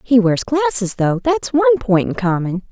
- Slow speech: No, average, 200 wpm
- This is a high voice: Yes, high, 225 Hz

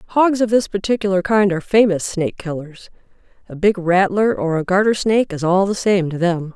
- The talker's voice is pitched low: No, high, 190 Hz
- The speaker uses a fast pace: No, average, 190 wpm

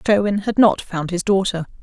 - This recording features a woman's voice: Yes, female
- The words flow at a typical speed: Yes, average, 195 wpm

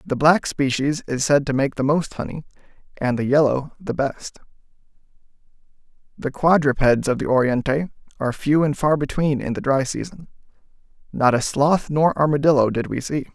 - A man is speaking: Yes, male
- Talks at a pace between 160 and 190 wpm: Yes, average, 165 wpm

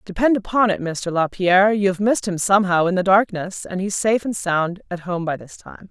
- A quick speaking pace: Yes, fast, 225 wpm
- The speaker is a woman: Yes, female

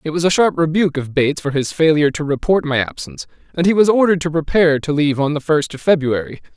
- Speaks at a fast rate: Yes, fast, 245 wpm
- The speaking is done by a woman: No, male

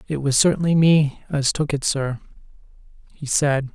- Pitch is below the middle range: No, medium, 145 Hz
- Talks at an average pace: Yes, average, 160 wpm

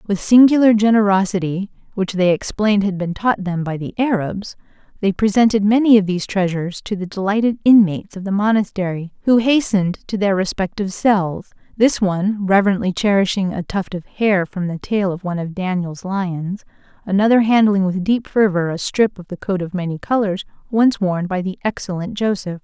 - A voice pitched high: Yes, high, 195 Hz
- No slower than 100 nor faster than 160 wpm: No, average, 175 wpm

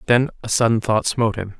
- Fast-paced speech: Yes, fast, 225 wpm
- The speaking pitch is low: Yes, low, 110 Hz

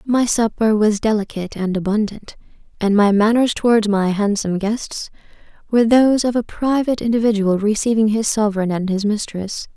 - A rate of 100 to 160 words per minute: Yes, average, 155 wpm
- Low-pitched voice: No, high, 215 Hz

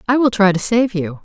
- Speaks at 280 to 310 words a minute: Yes, fast, 290 wpm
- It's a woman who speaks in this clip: Yes, female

